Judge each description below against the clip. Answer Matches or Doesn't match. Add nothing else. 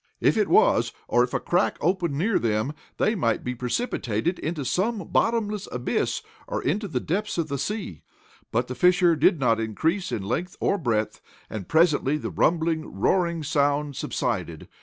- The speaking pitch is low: Doesn't match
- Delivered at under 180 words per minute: Matches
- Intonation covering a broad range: Matches